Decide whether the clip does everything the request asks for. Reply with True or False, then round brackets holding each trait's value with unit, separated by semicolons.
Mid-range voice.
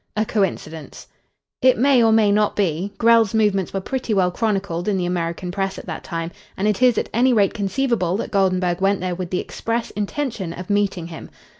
False (200 Hz)